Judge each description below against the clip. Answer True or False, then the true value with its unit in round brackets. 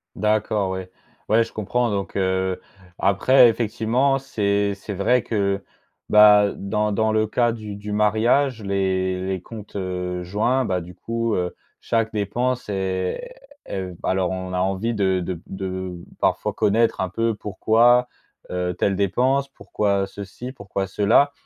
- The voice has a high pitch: False (100 Hz)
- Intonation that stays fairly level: False (3.3 semitones)